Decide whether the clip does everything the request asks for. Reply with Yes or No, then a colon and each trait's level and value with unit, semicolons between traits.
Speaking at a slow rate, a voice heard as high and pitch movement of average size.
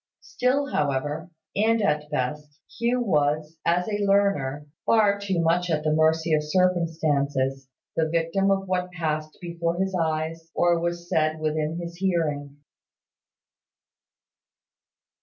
No: slow, 130 wpm; medium, 165 Hz; average, 3.2 semitones